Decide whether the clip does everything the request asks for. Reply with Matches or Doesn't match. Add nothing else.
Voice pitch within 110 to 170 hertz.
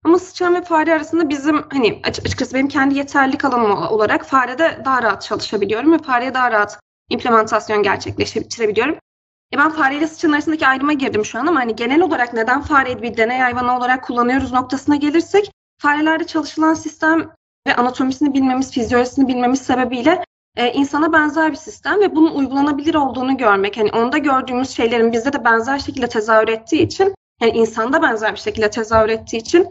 Doesn't match